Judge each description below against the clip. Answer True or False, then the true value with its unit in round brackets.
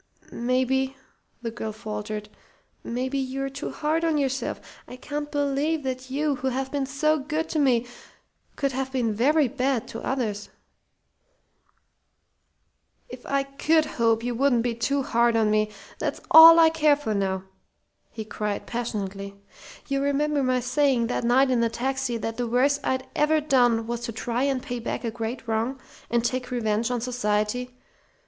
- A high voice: True (255 Hz)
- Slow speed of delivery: False (165 wpm)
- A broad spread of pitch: False (3.2 semitones)